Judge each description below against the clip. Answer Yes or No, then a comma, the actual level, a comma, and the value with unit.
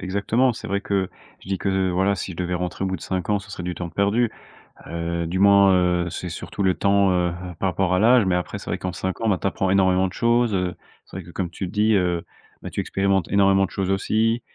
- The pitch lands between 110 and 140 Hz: No, very low, 95 Hz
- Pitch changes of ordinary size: No, narrow, 2.0 semitones